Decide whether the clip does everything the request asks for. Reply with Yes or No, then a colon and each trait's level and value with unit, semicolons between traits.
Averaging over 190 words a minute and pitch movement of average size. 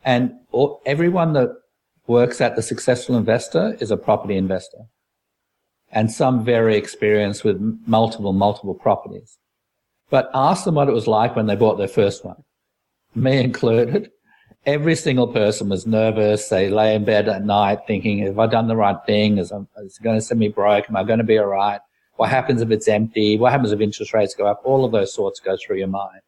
Yes: average, 200 wpm; average, 3.1 semitones